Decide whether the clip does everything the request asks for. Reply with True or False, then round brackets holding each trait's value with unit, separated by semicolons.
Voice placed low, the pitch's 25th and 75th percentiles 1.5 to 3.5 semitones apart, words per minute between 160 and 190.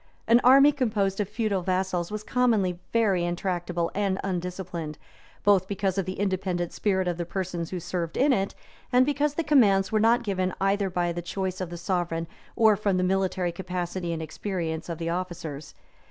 False (185 Hz; 2.8 semitones; 185 wpm)